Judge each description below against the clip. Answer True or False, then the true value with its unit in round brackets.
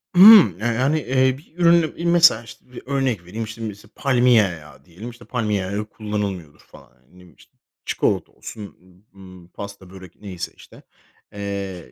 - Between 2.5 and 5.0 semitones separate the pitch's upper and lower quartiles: False (5.4 semitones)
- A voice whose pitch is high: False (105 Hz)